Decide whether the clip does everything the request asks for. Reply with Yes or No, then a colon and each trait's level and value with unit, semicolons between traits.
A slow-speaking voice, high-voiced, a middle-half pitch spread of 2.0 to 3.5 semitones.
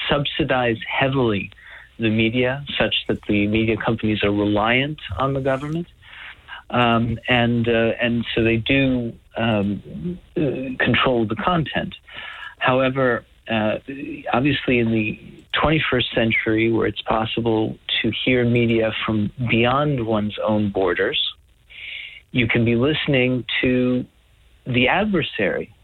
No: slow, 115 wpm; low, 120 Hz; average, 3.2 semitones